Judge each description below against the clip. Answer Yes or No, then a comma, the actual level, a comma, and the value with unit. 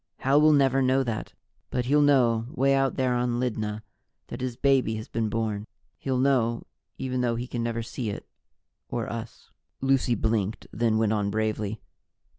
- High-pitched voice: No, low, 120 Hz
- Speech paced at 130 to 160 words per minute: No, average, 175 wpm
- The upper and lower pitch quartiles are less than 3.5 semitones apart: Yes, average, 3.0 semitones